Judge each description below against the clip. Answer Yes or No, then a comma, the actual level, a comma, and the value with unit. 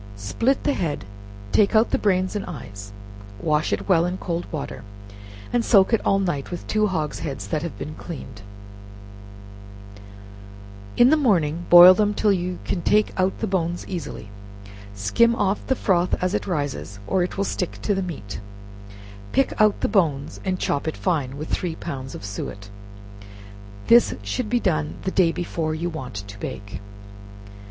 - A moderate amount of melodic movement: No, wide, 5.8 semitones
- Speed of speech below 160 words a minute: No, average, 170 wpm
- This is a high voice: No, medium, 175 Hz